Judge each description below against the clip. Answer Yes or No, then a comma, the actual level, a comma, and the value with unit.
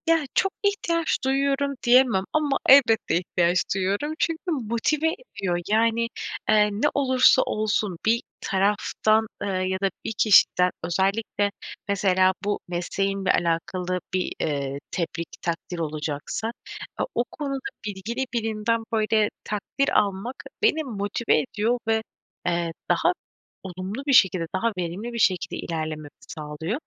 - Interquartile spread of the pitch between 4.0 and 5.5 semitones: Yes, average, 4.9 semitones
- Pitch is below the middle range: No, high, 210 Hz